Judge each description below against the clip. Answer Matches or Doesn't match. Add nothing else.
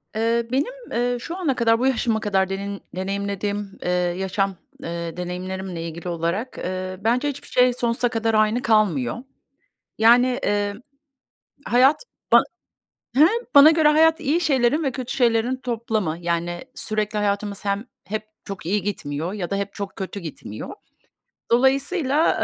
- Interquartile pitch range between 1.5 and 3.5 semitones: Doesn't match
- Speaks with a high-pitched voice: Matches